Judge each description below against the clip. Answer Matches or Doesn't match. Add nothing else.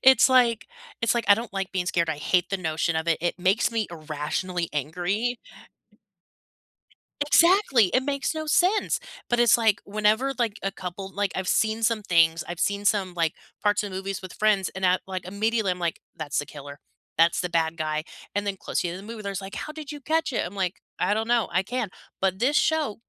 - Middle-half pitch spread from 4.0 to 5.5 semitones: Matches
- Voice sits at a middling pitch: Doesn't match